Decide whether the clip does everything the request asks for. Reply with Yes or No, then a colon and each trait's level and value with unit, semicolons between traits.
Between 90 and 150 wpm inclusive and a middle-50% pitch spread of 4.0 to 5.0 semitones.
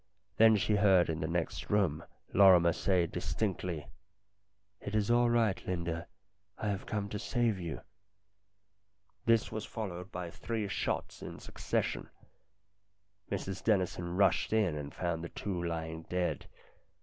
No: average, 140 wpm; average, 3.4 semitones